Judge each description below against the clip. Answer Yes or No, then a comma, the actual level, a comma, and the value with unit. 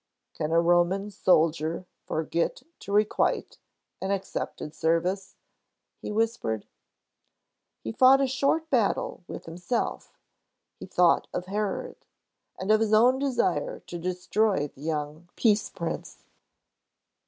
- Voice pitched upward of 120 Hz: Yes, high, 190 Hz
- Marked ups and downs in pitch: No, average, 4.7 semitones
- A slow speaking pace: Yes, slow, 120 wpm